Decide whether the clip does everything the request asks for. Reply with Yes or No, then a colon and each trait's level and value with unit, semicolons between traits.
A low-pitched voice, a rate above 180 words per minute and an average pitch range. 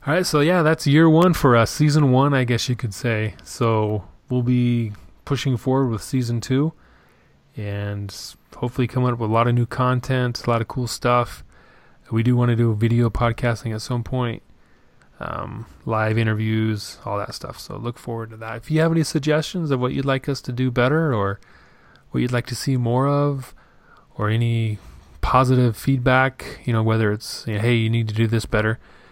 Yes: low, 120 Hz; average, 200 wpm; average, 3.0 semitones